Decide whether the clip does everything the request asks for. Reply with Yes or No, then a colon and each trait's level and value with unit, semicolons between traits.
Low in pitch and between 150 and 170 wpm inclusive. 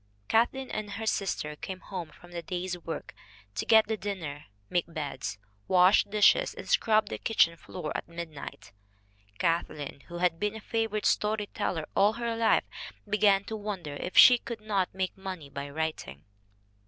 No: high, 190 Hz; average, 165 wpm